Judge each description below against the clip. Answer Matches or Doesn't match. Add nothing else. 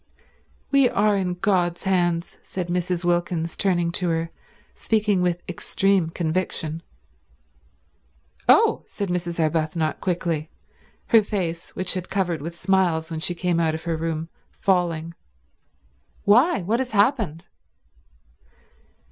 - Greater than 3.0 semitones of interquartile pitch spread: Doesn't match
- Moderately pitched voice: Matches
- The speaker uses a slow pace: Matches